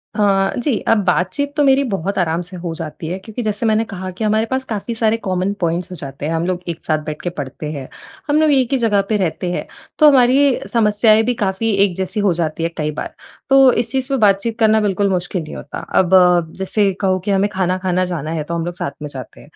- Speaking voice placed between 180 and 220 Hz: Yes, high, 190 Hz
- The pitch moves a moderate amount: Yes, average, 4.4 semitones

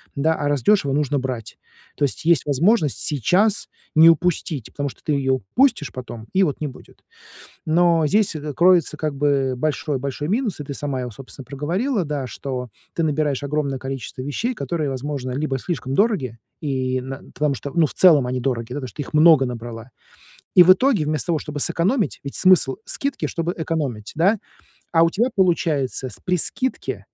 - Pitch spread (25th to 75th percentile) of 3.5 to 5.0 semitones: Yes, average, 4.2 semitones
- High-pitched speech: No, medium, 145 Hz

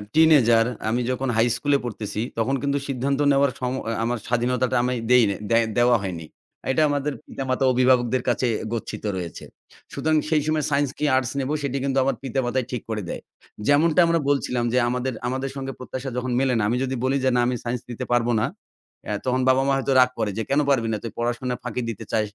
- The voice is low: Yes, low, 130 Hz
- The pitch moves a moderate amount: No, narrow, 2.2 semitones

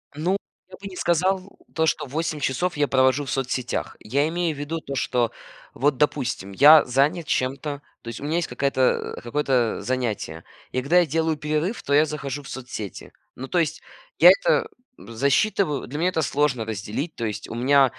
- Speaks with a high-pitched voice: No, medium, 145 Hz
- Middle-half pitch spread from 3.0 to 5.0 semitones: Yes, average, 3.9 semitones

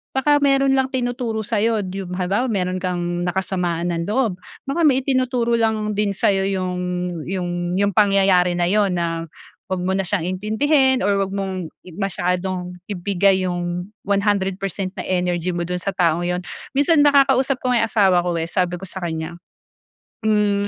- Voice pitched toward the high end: Yes, high, 195 Hz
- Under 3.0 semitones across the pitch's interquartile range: No, average, 3.5 semitones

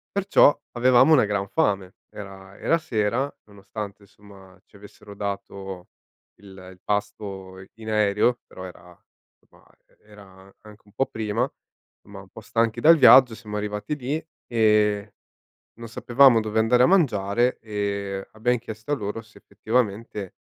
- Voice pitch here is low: Yes, low, 105 Hz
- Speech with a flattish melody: No, average, 3.1 semitones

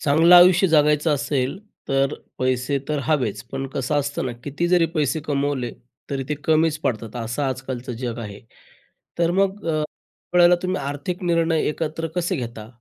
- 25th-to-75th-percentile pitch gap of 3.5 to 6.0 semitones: Yes, average, 4.2 semitones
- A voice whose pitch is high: No, medium, 145 Hz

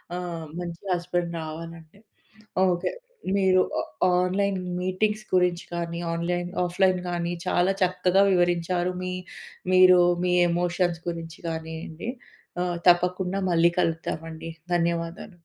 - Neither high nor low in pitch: Yes, medium, 175 Hz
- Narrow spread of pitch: Yes, narrow, 1.5 semitones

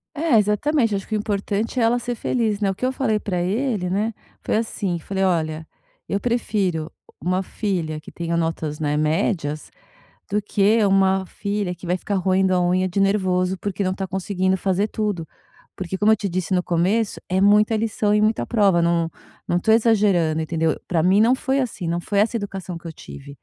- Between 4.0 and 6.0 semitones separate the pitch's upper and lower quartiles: No, average, 3.3 semitones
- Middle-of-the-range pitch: No, high, 195 Hz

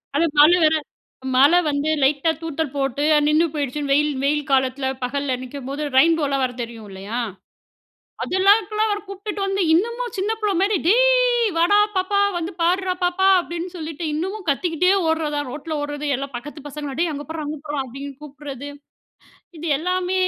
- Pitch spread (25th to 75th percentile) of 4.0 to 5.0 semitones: Yes, average, 4.7 semitones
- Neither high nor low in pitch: No, very high, 310 Hz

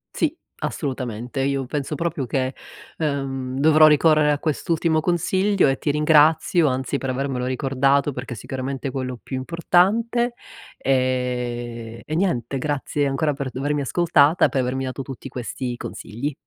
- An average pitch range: Yes, average, 3.2 semitones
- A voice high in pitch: No, medium, 140 Hz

